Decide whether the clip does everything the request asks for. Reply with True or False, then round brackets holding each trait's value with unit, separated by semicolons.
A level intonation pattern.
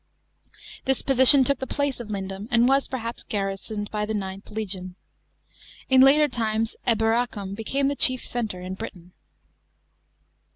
False (4.6 semitones)